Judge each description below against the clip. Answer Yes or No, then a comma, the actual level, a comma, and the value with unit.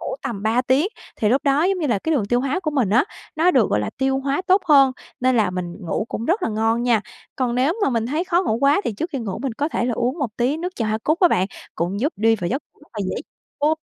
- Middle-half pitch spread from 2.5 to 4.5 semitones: No, average, 5.3 semitones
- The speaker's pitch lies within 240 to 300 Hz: Yes, very high, 255 Hz